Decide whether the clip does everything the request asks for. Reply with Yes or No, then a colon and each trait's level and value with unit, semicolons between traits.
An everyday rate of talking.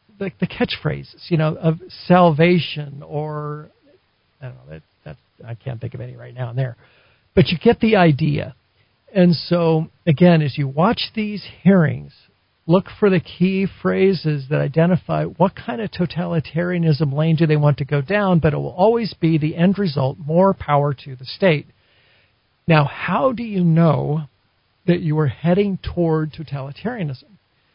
Yes: average, 165 wpm